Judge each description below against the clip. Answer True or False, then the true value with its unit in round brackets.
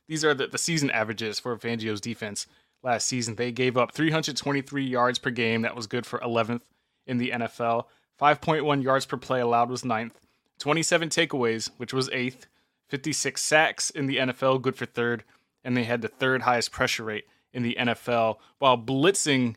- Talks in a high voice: False (125 Hz)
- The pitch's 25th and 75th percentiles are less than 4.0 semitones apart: True (2.7 semitones)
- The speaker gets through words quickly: False (180 wpm)